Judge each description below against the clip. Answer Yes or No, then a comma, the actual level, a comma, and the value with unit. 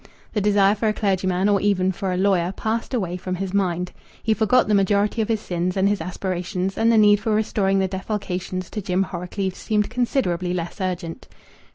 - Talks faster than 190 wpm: Yes, average, 200 wpm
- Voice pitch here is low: No, high, 195 Hz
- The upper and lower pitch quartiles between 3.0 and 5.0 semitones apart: No, narrow, 2.5 semitones